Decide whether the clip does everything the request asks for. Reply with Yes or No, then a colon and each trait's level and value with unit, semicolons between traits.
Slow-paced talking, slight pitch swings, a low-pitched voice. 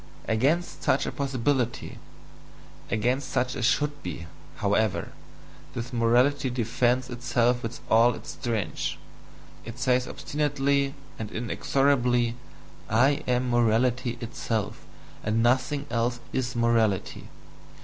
Yes: slow, 110 wpm; narrow, 2.3 semitones; low, 125 Hz